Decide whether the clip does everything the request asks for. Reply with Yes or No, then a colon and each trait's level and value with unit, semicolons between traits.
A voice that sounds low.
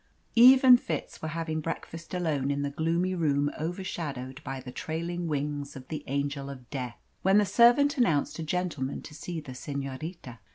No: medium, 155 Hz